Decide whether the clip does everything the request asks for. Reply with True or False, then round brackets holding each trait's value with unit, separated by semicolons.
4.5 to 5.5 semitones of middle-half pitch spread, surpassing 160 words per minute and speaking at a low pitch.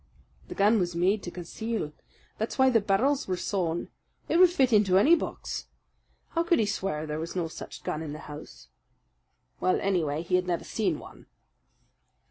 False (5.0 semitones; 180 wpm; 190 Hz)